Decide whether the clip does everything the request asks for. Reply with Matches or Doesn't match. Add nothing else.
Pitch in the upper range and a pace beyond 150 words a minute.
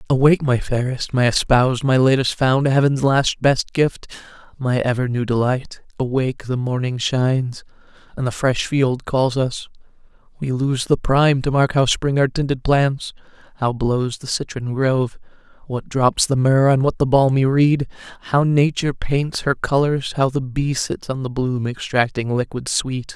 Doesn't match